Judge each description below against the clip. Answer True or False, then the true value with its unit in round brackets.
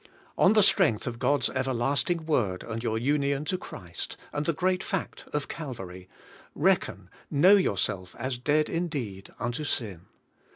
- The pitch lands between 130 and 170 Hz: True (135 Hz)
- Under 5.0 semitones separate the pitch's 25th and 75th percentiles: False (5.6 semitones)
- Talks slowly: False (150 wpm)